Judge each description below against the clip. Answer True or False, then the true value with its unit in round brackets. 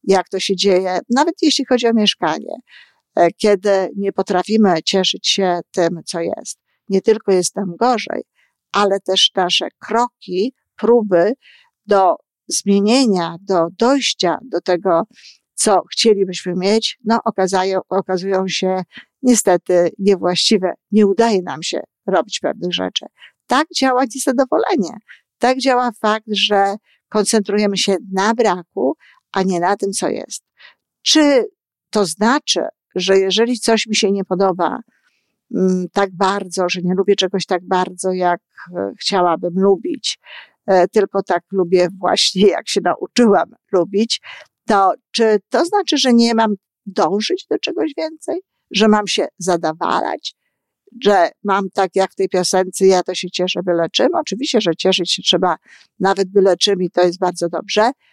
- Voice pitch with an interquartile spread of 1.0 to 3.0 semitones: False (3.7 semitones)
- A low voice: False (195 Hz)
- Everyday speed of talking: True (140 wpm)